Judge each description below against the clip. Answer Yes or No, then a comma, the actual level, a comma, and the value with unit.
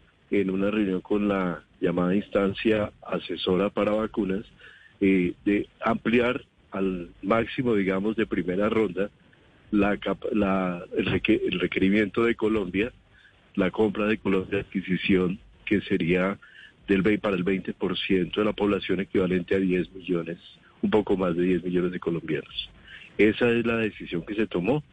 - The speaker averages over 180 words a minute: No, average, 150 wpm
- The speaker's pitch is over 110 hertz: No, low, 100 Hz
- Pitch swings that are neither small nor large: No, narrow, 2.3 semitones